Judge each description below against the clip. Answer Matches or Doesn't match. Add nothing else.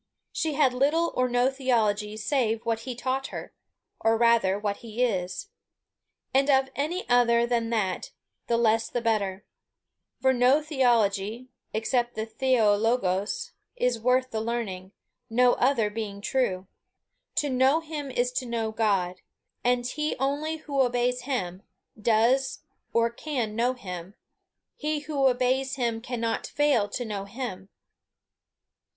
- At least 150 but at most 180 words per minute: Doesn't match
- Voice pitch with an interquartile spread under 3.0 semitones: Doesn't match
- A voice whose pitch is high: Matches